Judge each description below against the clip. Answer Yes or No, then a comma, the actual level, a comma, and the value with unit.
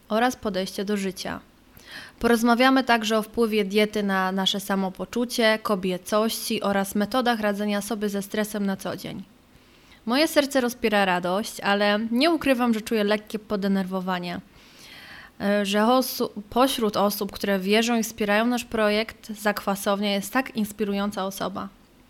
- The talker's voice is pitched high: Yes, high, 210 Hz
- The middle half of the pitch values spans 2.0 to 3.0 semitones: Yes, narrow, 2.6 semitones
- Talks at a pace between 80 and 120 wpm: No, average, 130 wpm